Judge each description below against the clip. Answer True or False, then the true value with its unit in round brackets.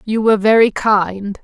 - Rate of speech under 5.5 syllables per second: True (4.5 syllables/s)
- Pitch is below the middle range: False (210 Hz)